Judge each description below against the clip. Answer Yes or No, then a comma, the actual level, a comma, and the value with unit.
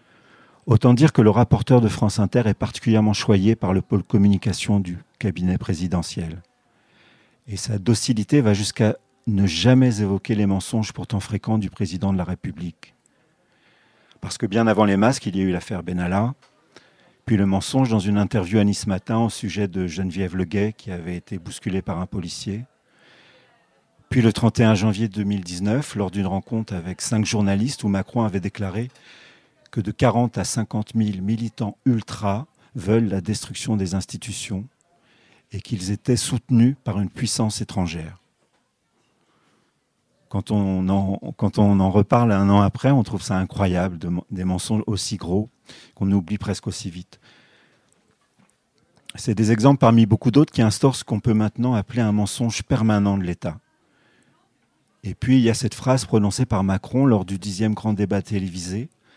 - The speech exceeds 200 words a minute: No, average, 165 wpm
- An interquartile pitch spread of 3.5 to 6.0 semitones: No, average, 2.9 semitones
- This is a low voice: Yes, low, 105 Hz